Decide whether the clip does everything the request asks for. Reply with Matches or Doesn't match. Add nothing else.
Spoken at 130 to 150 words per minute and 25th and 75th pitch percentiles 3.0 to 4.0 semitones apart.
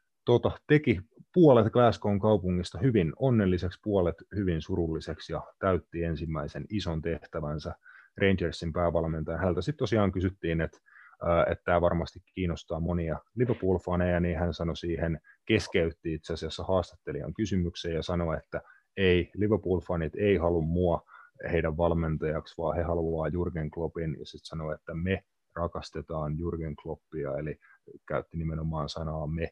Doesn't match